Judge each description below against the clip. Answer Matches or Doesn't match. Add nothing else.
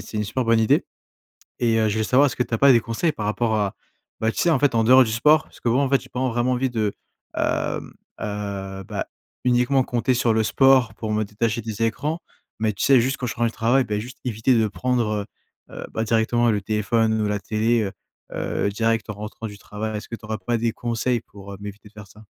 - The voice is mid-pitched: Doesn't match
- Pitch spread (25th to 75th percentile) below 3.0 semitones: Matches